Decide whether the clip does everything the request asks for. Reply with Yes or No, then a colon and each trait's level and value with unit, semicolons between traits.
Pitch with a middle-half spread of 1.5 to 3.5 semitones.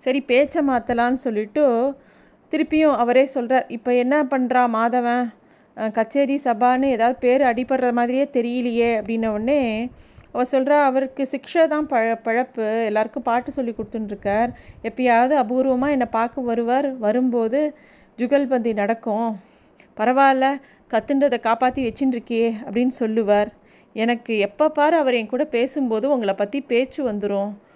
Yes: average, 3.0 semitones